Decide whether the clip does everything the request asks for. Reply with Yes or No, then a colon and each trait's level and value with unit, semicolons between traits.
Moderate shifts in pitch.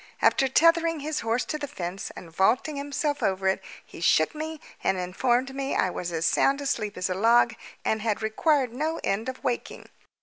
No: wide, 7.0 semitones